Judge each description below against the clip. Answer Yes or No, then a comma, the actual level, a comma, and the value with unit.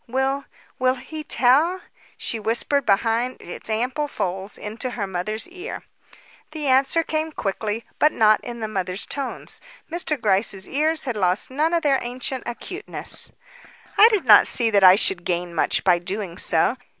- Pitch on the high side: Yes, high, 240 Hz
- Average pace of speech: Yes, average, 160 wpm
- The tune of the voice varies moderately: No, wide, 6.0 semitones